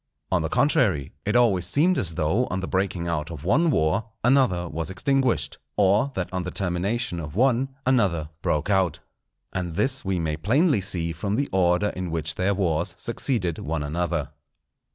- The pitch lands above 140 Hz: No, very low, 95 Hz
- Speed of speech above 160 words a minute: Yes, average, 175 wpm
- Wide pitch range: Yes, wide, 5.9 semitones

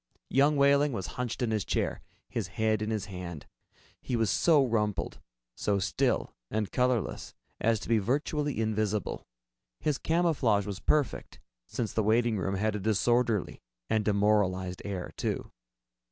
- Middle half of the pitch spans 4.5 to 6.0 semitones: No, average, 3.6 semitones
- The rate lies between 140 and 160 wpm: Yes, average, 150 wpm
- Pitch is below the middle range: Yes, low, 110 Hz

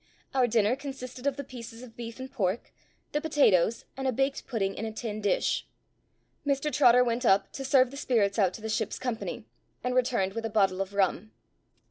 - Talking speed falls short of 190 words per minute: No, average, 200 wpm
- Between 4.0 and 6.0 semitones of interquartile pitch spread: No, average, 3.6 semitones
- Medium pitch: No, high, 235 Hz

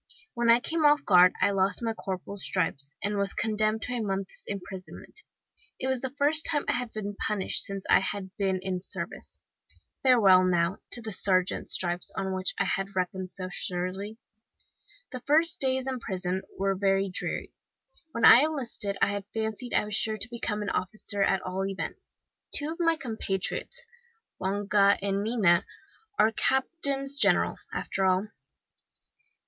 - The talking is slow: No, average, 165 wpm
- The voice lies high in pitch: Yes, high, 200 Hz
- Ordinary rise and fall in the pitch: Yes, average, 4.1 semitones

